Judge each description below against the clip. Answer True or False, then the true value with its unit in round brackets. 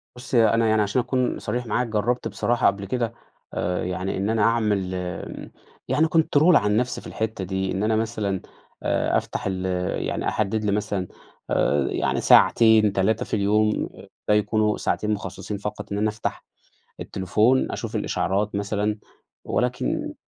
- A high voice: False (105 Hz)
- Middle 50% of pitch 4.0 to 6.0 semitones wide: False (2.5 semitones)